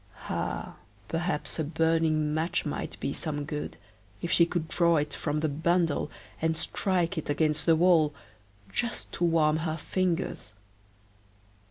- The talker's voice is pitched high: No, medium, 160 Hz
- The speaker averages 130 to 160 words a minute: Yes, average, 145 wpm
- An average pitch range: No, narrow, 1.9 semitones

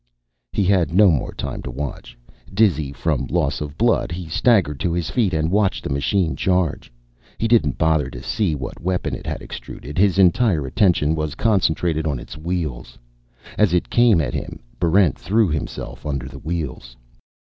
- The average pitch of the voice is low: Yes, very low, 85 Hz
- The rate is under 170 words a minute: No, average, 175 wpm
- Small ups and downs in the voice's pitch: No, average, 4.8 semitones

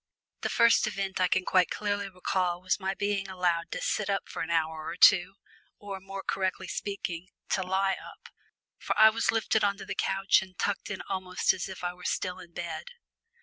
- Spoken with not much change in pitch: Yes, narrow, 1.7 semitones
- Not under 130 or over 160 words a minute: No, fast, 205 wpm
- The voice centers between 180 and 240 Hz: Yes, high, 190 Hz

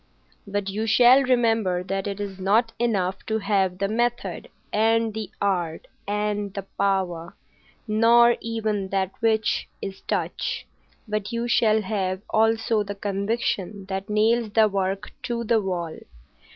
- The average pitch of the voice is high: Yes, high, 210 Hz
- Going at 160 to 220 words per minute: No, average, 140 wpm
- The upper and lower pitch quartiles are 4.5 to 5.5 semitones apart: No, narrow, 2.6 semitones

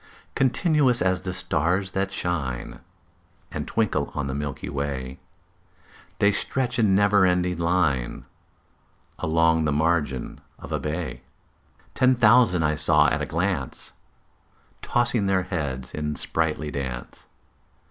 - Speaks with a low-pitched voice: Yes, very low, 85 Hz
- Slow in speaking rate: Yes, slow, 125 wpm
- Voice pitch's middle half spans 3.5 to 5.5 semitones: Yes, average, 5.0 semitones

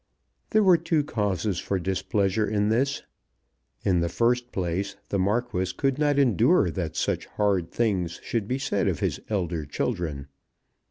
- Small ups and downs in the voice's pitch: No, average, 4.9 semitones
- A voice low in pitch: Yes, low, 100 Hz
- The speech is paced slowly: No, average, 155 wpm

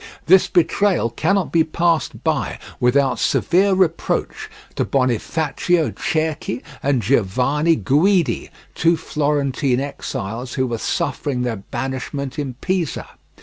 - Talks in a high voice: No, medium, 145 Hz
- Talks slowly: Yes, slow, 110 wpm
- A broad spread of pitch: No, average, 4.8 semitones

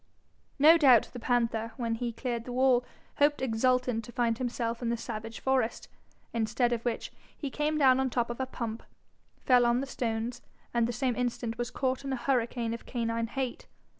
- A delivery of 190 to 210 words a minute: Yes, average, 195 wpm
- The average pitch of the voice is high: Yes, high, 240 Hz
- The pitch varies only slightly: Yes, narrow, 2.0 semitones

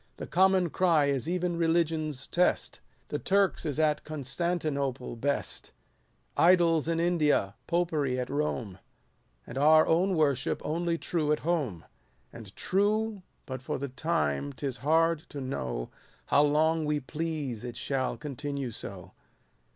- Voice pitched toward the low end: No, medium, 150 Hz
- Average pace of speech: Yes, average, 145 wpm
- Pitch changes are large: No, average, 3.7 semitones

